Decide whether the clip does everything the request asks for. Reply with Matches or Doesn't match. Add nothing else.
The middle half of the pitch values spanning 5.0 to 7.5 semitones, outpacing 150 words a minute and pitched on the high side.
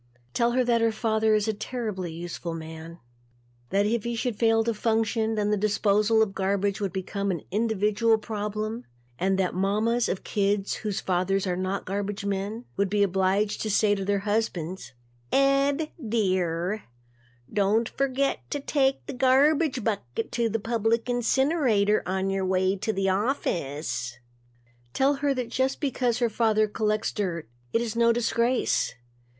Doesn't match